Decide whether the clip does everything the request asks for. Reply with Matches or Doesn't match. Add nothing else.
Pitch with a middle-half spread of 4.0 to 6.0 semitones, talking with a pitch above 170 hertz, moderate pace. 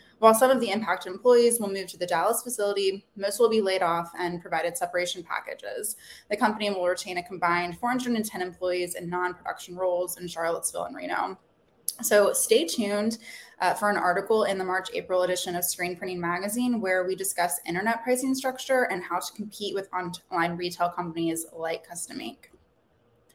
Doesn't match